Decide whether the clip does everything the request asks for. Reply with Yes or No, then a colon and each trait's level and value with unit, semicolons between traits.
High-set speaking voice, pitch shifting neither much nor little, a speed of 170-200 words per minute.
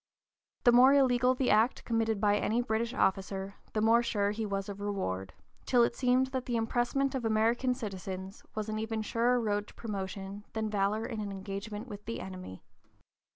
Yes: high, 220 Hz; average, 3.1 semitones; average, 185 wpm